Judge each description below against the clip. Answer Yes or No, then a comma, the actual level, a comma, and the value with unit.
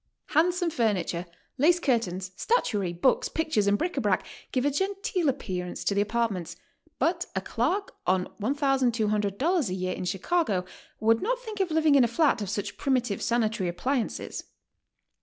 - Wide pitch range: Yes, wide, 8.1 semitones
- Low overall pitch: No, high, 235 Hz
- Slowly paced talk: No, average, 165 wpm